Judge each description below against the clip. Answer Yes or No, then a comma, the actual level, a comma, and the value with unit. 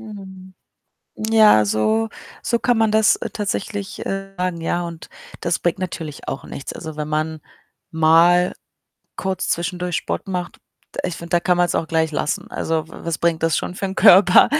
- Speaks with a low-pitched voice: No, medium, 175 Hz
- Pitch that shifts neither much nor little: Yes, average, 3.2 semitones